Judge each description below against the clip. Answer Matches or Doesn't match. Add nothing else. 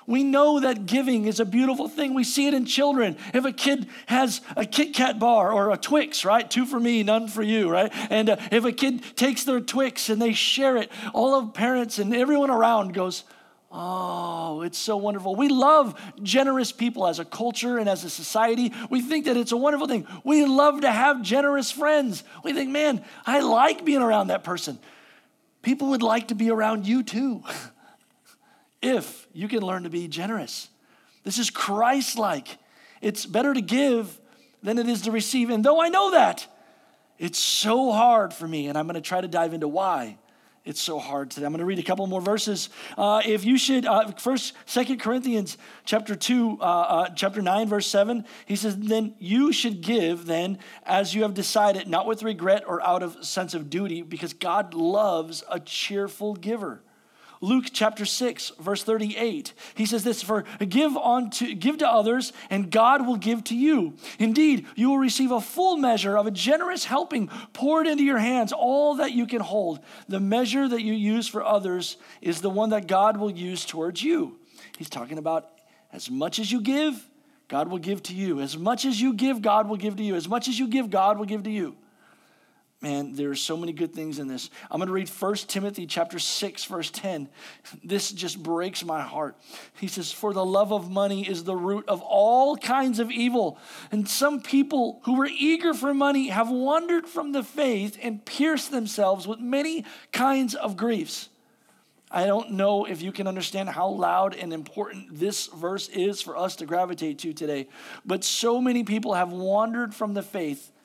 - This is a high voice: Matches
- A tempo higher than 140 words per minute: Matches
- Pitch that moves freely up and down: Doesn't match